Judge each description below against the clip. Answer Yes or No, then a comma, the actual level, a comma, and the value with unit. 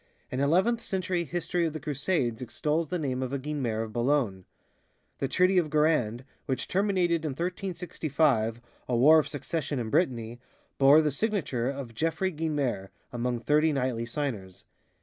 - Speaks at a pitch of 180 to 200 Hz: No, medium, 145 Hz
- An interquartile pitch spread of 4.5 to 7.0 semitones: Yes, average, 5.1 semitones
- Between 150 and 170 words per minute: Yes, average, 155 wpm